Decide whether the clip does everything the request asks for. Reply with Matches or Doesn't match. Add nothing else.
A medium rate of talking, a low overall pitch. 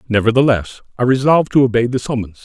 Matches